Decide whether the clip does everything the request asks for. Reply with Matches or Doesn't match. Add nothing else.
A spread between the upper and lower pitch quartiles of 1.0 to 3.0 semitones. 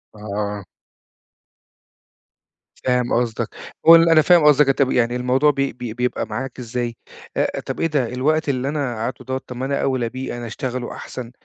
Matches